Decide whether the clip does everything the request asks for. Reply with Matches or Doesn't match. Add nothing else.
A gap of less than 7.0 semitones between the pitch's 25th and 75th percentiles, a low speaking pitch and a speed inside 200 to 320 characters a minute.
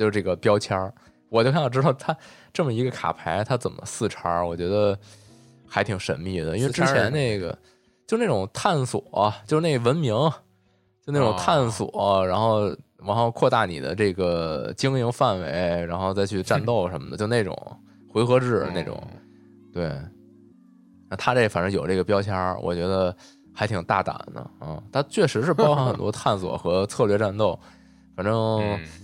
Matches